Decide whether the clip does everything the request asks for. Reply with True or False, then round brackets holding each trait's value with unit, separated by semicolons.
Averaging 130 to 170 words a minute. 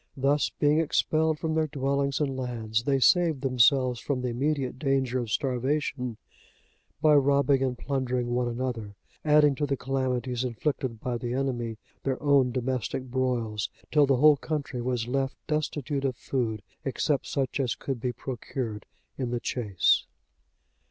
True (150 wpm)